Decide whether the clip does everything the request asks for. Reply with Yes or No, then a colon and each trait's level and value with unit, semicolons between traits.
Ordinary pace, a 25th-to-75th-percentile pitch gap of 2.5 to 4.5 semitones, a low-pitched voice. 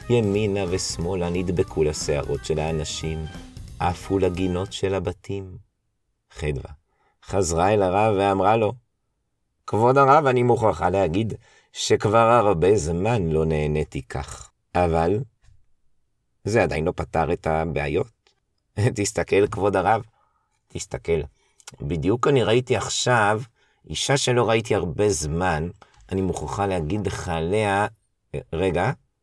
Yes: average, 110 wpm; average, 4.2 semitones; low, 100 Hz